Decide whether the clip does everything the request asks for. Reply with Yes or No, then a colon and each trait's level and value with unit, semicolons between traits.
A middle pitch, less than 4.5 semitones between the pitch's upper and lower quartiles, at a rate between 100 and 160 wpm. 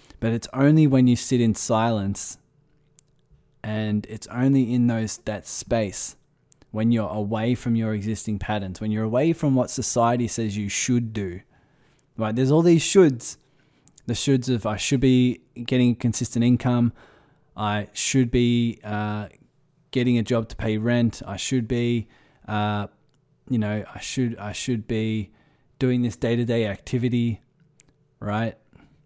No: low, 120 Hz; average, 3.5 semitones; average, 155 wpm